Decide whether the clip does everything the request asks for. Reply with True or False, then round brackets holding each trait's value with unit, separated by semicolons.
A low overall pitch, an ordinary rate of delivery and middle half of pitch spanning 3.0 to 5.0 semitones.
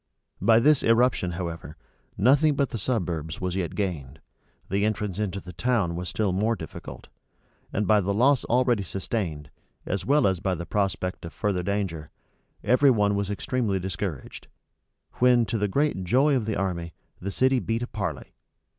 True (100 Hz; 170 wpm; 4.7 semitones)